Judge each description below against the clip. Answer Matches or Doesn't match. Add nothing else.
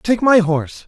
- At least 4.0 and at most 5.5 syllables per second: Matches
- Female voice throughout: Doesn't match